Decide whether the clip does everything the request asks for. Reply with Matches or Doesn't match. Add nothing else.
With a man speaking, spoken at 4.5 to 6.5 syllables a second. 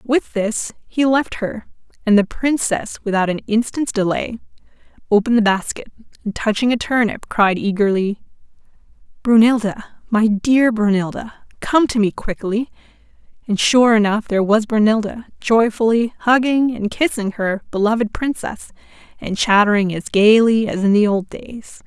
Doesn't match